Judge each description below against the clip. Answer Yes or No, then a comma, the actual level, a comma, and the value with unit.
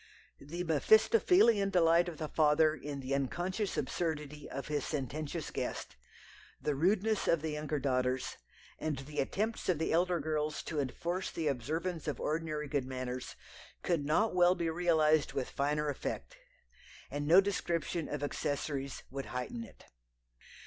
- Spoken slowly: No, average, 150 wpm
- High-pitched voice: No, medium, 155 Hz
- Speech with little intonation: No, average, 3.5 semitones